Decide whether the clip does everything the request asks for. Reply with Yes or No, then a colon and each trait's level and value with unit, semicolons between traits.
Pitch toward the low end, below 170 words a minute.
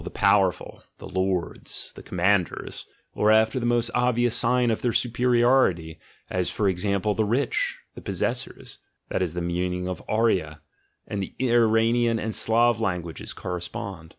Yes: low, 105 Hz; average, 150 wpm